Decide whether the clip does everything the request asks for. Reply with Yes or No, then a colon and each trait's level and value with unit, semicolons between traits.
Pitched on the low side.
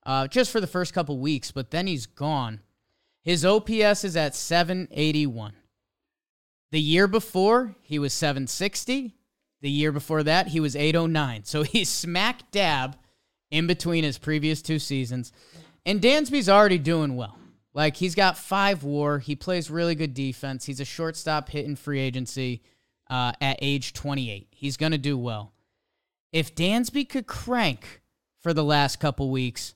No: medium, 150 Hz